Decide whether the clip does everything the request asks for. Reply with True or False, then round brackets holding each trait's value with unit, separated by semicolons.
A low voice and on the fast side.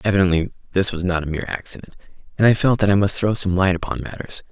True (95 Hz; 225 wpm)